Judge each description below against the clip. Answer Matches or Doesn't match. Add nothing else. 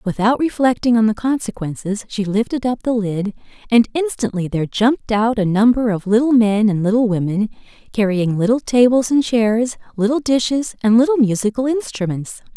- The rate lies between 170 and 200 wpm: Doesn't match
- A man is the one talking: Doesn't match